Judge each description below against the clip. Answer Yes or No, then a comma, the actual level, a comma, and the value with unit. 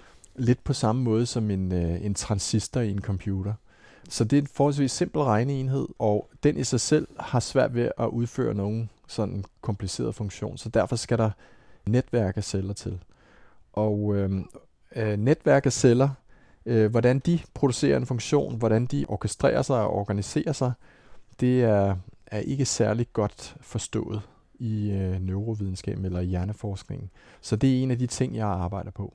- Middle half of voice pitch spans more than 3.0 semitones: Yes, average, 3.9 semitones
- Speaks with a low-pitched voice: Yes, low, 110 Hz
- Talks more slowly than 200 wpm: Yes, average, 165 wpm